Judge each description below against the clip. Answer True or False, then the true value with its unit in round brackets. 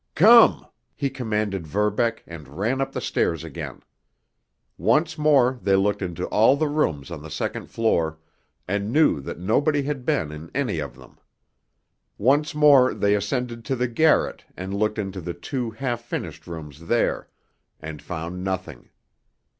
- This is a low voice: True (105 Hz)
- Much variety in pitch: True (7.7 semitones)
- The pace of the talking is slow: False (155 wpm)